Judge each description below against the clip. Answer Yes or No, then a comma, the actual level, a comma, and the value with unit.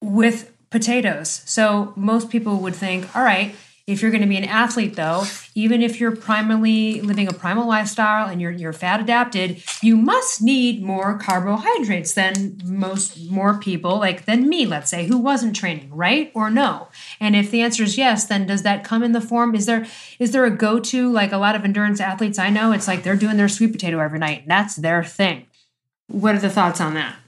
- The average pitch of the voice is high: Yes, high, 210 Hz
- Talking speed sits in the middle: No, fast, 210 wpm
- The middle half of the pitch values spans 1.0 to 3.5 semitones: Yes, average, 3.2 semitones